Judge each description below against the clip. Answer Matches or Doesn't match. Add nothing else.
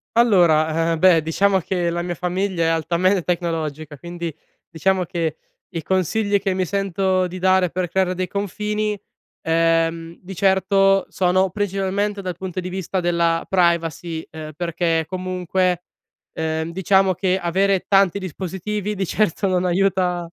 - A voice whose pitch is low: Doesn't match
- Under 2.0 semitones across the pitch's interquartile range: Doesn't match